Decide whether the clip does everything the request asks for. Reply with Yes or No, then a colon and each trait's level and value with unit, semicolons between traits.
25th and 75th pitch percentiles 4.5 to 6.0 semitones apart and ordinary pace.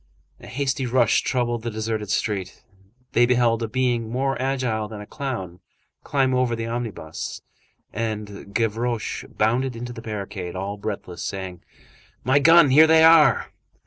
No: average, 3.5 semitones; average, 145 wpm